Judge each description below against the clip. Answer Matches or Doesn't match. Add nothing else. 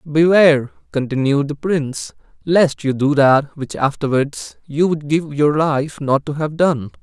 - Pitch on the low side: Doesn't match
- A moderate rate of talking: Matches